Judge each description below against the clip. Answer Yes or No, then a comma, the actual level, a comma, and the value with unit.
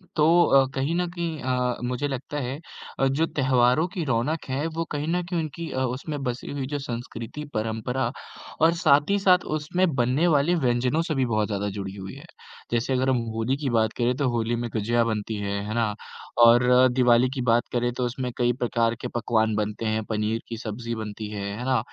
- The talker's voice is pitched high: No, low, 125 Hz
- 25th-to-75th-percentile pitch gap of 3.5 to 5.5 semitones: Yes, average, 3.9 semitones